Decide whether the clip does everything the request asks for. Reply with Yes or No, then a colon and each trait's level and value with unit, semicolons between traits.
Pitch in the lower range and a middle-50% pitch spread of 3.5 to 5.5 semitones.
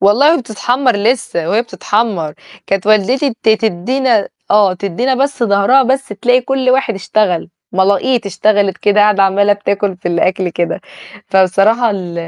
No: high, 205 Hz; average, 4.2 semitones